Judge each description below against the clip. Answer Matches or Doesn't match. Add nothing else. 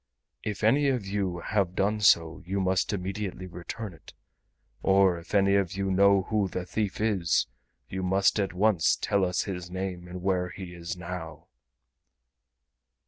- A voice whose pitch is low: Matches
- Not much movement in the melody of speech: Matches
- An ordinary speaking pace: Matches